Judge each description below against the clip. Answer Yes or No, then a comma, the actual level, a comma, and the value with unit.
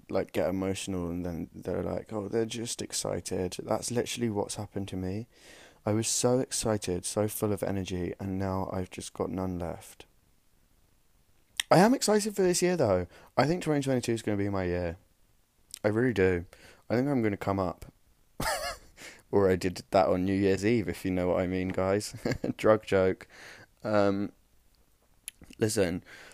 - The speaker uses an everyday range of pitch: Yes, average, 3.5 semitones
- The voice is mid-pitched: No, low, 100 Hz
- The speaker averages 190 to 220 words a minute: No, average, 175 wpm